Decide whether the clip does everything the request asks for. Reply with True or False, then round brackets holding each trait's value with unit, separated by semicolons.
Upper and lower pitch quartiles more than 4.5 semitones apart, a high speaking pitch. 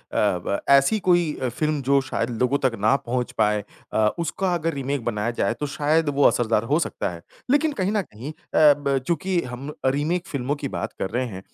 False (5.0 semitones; 140 Hz)